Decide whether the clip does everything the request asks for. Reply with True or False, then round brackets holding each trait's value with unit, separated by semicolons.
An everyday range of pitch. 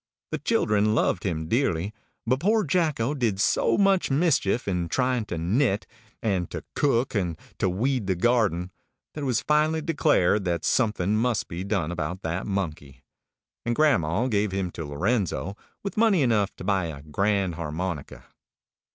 False (6.5 semitones)